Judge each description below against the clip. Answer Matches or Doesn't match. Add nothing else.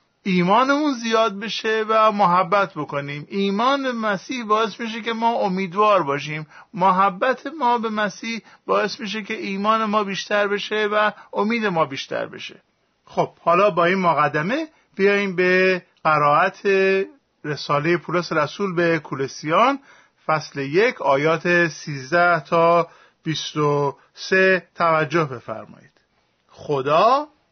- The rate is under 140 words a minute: Matches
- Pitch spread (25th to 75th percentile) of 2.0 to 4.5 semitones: Doesn't match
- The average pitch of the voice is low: Doesn't match